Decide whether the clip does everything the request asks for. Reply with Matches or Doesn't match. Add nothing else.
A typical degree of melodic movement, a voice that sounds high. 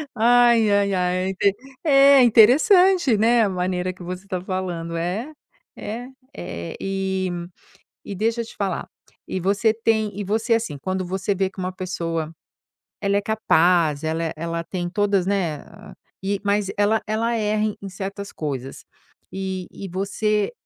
Matches